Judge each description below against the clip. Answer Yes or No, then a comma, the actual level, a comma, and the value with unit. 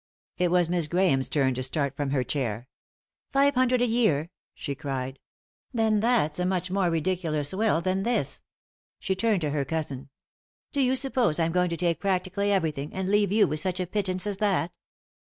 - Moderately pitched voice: Yes, medium, 180 Hz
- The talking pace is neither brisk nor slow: No, fast, 215 wpm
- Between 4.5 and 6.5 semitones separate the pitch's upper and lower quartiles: Yes, wide, 5.4 semitones